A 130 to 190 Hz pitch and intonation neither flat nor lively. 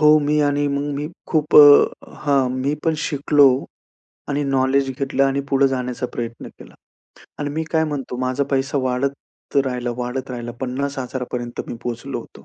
No: low, 135 Hz; narrow, 2.2 semitones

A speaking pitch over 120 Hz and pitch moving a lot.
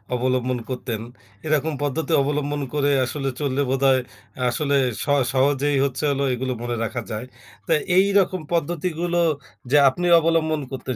No: medium, 140 Hz; average, 3.3 semitones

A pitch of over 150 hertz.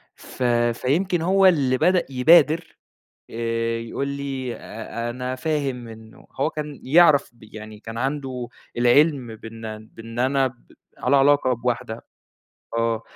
No: low, 130 Hz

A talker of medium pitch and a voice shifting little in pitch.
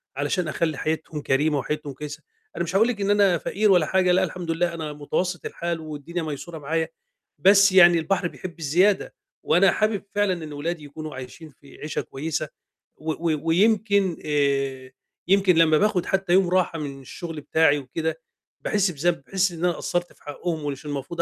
No: medium, 165 Hz; average, 3.6 semitones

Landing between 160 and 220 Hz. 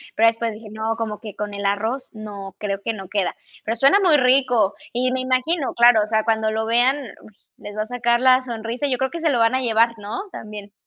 No: high, 230 Hz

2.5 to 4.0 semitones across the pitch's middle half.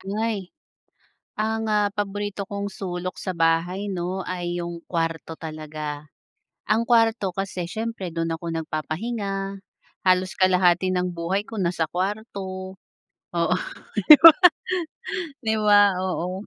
Yes: average, 3.1 semitones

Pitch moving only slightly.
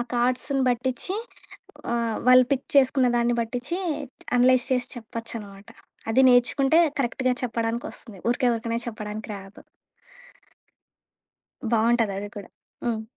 Yes: narrow, 2.2 semitones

